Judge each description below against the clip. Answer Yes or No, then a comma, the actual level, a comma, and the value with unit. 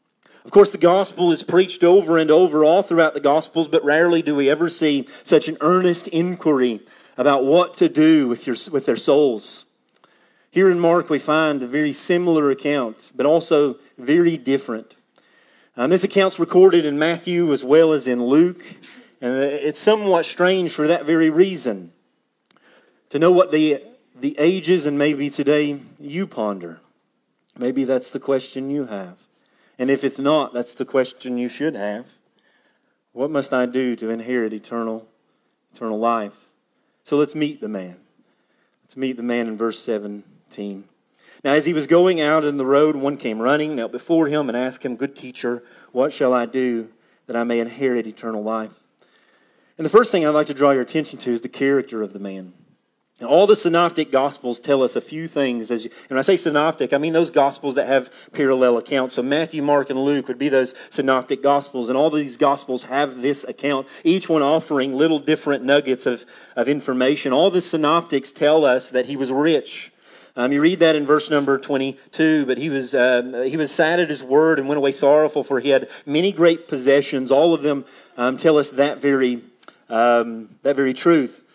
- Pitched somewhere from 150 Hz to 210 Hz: No, medium, 140 Hz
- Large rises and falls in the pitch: No, average, 3.9 semitones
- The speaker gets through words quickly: No, average, 190 wpm